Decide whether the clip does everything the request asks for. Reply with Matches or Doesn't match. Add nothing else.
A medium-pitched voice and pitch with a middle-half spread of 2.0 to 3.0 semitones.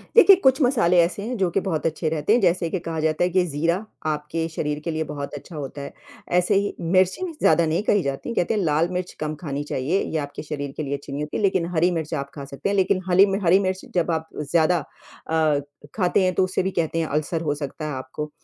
Doesn't match